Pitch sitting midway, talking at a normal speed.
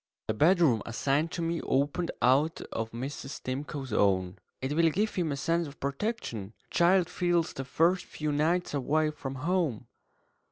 Yes: medium, 150 Hz; average, 165 wpm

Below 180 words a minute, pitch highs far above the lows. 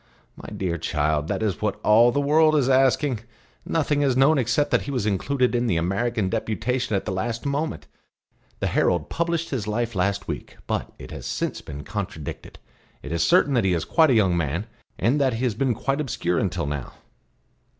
No: average, 195 wpm; wide, 6.5 semitones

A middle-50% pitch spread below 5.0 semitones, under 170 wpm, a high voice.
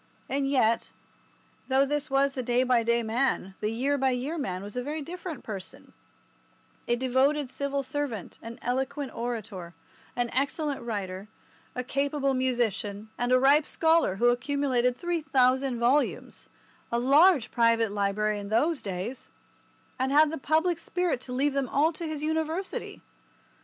Yes: average, 3.7 semitones; average, 145 wpm; very high, 260 Hz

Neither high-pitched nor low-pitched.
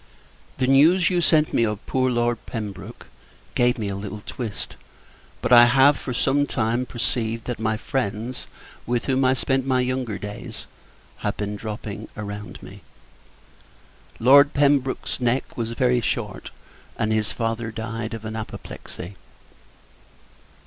No: low, 120 Hz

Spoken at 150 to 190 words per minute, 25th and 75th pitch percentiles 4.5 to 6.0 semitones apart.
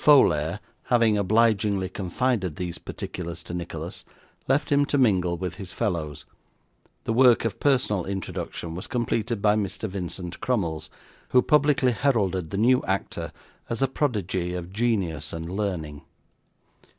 No: average, 140 wpm; average, 5.2 semitones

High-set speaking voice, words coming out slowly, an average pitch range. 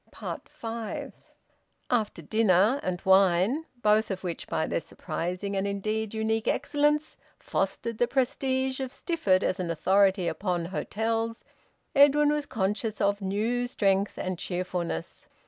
Yes: high, 210 Hz; slow, 130 wpm; average, 4.5 semitones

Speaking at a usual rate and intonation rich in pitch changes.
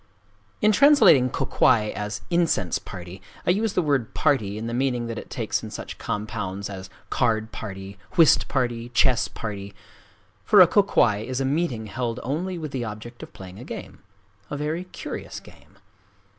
Yes: average, 170 wpm; wide, 6.0 semitones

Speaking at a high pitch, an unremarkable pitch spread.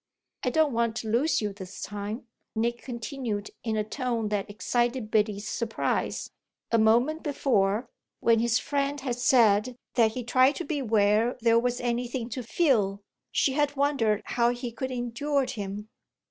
Yes: high, 235 Hz; average, 3.0 semitones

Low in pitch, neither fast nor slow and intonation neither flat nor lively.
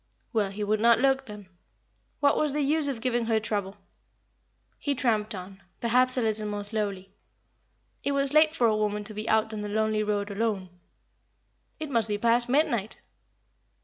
No: high, 220 Hz; average, 180 wpm; average, 3.5 semitones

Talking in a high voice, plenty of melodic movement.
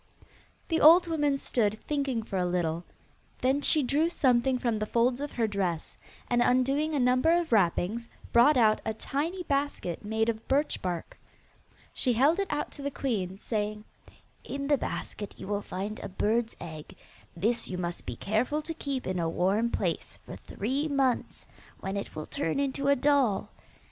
Yes: high, 240 Hz; wide, 5.7 semitones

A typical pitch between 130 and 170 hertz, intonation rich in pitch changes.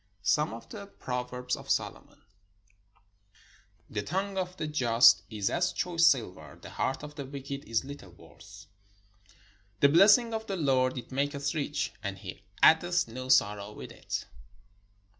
Yes: medium, 140 Hz; wide, 6.2 semitones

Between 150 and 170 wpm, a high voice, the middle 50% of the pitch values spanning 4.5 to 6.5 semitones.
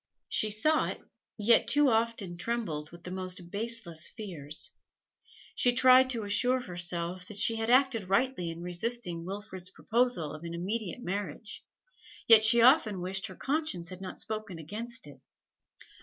Yes: average, 155 wpm; high, 205 Hz; average, 5.0 semitones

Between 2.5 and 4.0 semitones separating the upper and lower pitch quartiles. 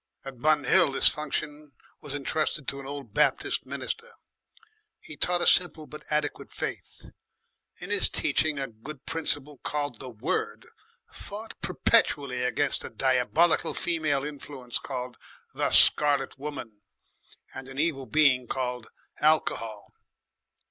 Yes: average, 2.9 semitones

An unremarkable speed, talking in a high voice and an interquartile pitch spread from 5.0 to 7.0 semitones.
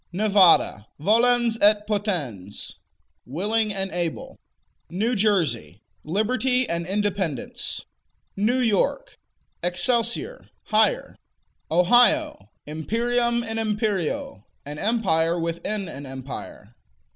No: slow, 85 wpm; high, 205 Hz; wide, 5.6 semitones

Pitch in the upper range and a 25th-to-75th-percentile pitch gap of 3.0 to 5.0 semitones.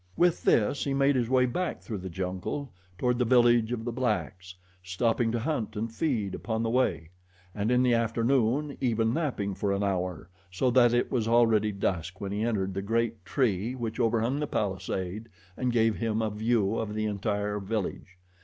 No: low, 115 Hz; average, 3.4 semitones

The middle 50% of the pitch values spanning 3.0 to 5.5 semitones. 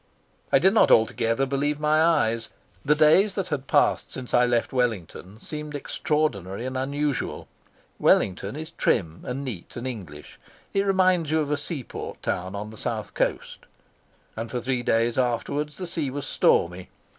Yes: average, 5.0 semitones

